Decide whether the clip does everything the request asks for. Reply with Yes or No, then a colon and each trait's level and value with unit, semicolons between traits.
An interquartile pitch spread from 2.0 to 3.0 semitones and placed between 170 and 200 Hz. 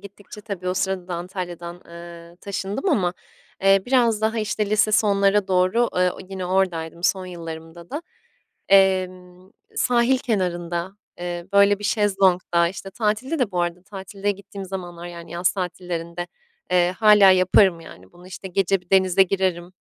Yes: narrow, 2.4 semitones; medium, 185 Hz